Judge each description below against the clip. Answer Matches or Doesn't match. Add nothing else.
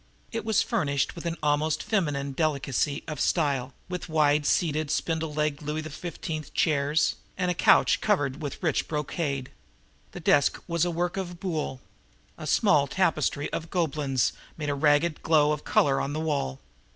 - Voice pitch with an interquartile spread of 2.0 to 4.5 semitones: Matches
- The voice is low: Doesn't match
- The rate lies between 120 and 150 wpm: Doesn't match